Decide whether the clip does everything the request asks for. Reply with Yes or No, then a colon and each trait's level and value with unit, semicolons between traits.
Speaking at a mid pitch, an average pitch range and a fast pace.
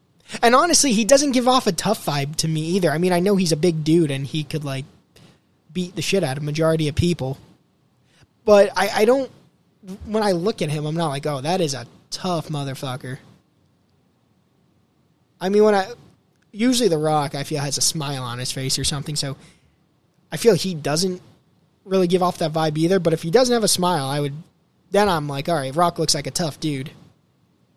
Yes: medium, 165 Hz; average, 4.2 semitones; fast, 210 wpm